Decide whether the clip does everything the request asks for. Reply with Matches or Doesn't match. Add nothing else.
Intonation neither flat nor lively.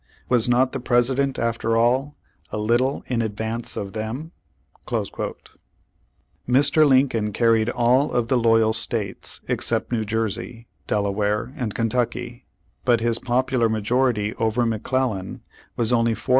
Doesn't match